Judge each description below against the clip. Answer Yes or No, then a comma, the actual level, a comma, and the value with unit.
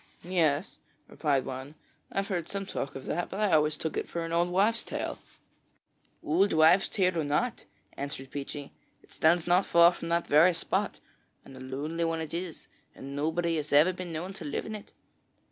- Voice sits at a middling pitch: Yes, medium, 165 Hz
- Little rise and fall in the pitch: No, average, 3.5 semitones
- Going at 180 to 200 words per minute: Yes, average, 195 wpm